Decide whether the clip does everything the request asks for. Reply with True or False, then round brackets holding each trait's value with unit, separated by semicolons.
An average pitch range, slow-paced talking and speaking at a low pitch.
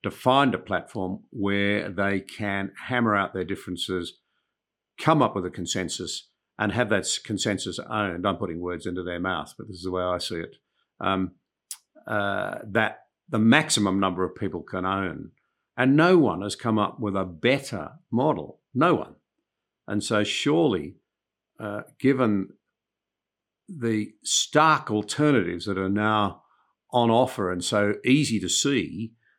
False (3.3 semitones; 155 wpm; 100 Hz)